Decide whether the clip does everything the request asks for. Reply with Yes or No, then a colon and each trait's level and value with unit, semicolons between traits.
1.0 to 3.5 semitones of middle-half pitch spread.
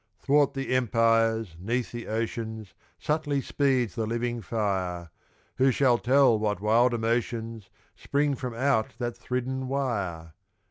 Yes: average, 2.9 semitones